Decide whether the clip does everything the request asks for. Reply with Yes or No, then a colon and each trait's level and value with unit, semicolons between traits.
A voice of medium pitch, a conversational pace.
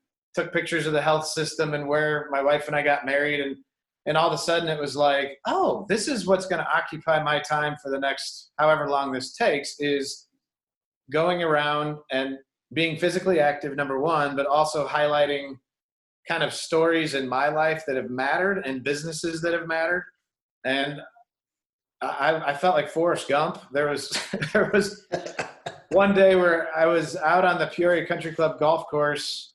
Yes: medium, 150 Hz; average, 180 wpm